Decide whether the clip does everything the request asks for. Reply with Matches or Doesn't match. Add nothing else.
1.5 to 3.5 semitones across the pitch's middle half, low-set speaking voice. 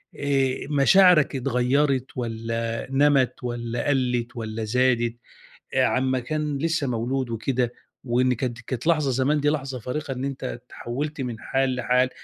Matches